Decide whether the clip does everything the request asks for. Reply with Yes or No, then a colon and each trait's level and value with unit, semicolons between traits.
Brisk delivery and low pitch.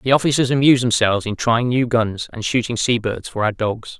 Yes: fast, 225 wpm; low, 120 Hz